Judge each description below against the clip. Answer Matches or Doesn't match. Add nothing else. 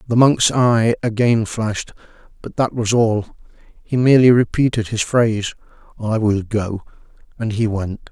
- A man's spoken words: Matches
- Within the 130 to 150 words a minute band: Matches